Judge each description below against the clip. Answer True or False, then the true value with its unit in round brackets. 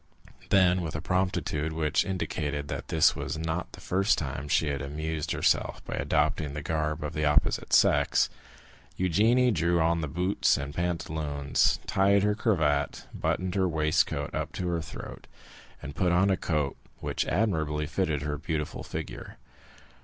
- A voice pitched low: True (80 Hz)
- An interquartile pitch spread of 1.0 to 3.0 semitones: False (3.6 semitones)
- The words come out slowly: False (160 wpm)